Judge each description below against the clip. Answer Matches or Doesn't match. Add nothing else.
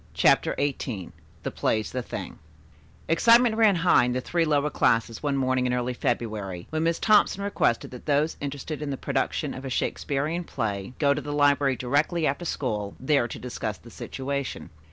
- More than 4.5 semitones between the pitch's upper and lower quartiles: Doesn't match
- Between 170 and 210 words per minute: Matches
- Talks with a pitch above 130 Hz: Matches